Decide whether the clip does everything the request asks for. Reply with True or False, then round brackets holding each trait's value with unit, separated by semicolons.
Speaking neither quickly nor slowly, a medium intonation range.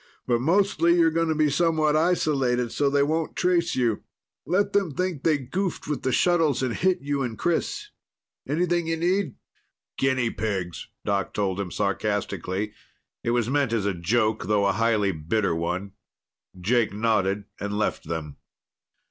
False (160 wpm; 7.9 semitones)